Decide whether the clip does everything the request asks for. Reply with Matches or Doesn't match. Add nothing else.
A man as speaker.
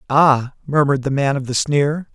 Matches